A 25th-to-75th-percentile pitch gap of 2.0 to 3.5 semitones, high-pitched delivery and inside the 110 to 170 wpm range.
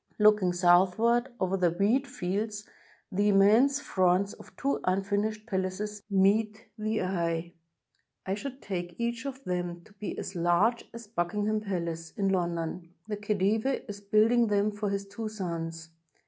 Yes: average, 3.2 semitones; high, 200 Hz; average, 150 wpm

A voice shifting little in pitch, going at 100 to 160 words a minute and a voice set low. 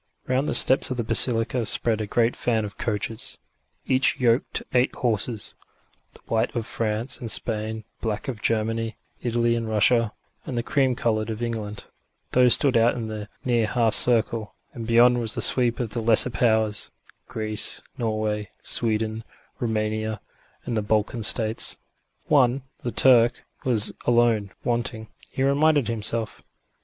Yes: narrow, 2.0 semitones; average, 155 wpm; low, 115 Hz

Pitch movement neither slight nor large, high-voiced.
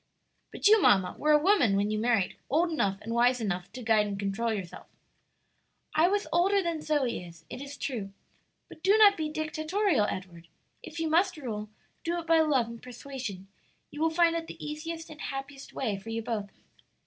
No: wide, 7.4 semitones; very high, 270 Hz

